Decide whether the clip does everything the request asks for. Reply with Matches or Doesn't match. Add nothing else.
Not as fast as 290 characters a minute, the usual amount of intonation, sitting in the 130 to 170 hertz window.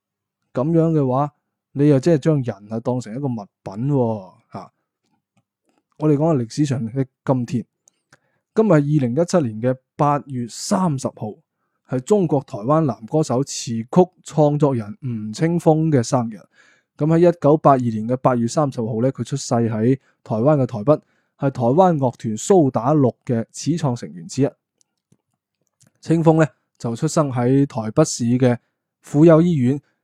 Matches